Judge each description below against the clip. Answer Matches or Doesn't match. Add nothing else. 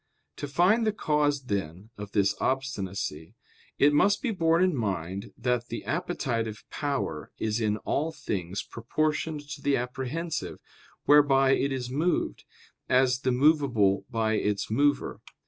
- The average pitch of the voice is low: Matches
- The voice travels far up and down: Matches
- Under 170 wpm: Matches